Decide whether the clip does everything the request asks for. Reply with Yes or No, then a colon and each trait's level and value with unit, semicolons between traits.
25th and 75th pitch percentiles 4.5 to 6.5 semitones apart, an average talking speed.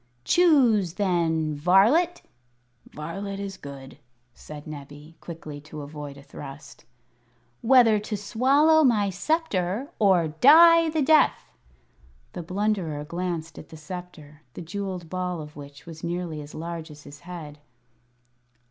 No: wide, 5.6 semitones; slow, 130 wpm